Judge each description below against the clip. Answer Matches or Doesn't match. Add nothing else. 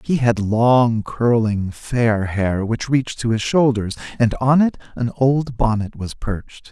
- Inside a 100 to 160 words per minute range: Doesn't match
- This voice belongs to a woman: Doesn't match